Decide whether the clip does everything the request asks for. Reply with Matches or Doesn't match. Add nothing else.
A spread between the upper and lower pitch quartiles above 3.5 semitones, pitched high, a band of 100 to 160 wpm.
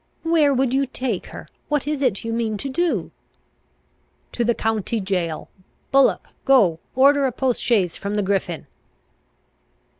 Matches